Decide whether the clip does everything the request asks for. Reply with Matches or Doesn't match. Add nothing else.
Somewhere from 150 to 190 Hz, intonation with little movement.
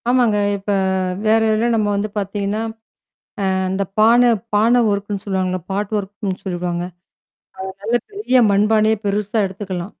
Doesn't match